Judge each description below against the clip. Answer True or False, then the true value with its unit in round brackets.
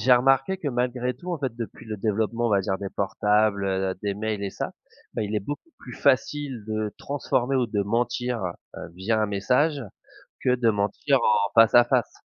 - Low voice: True (115 Hz)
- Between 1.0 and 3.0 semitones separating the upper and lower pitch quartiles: False (3.7 semitones)